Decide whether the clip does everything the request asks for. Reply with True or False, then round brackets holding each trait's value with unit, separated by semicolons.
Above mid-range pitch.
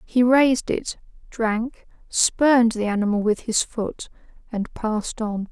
True (230 Hz)